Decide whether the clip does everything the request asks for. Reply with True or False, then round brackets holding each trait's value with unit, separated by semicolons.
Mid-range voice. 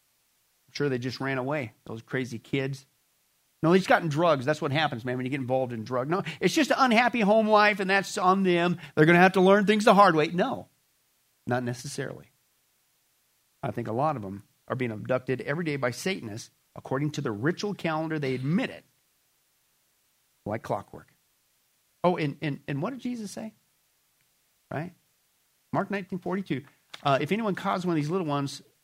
True (150 Hz)